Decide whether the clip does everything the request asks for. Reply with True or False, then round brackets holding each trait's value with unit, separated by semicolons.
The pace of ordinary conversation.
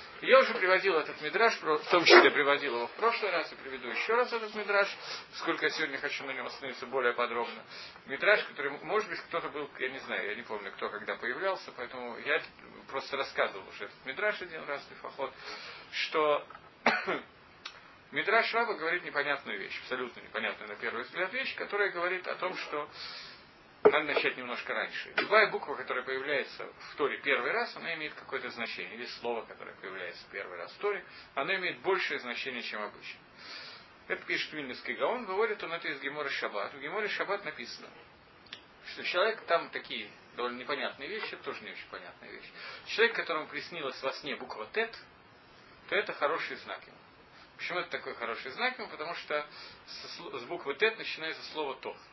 False (175 wpm)